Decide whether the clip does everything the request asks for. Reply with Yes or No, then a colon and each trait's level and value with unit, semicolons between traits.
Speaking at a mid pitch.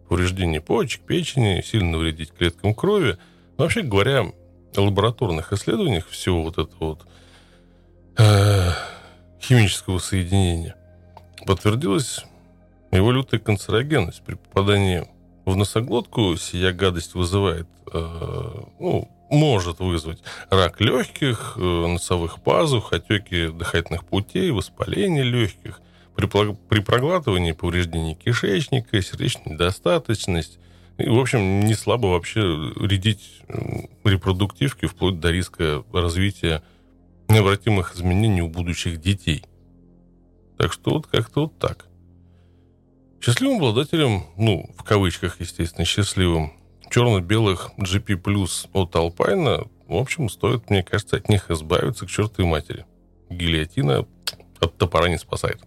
No: very low, 95 Hz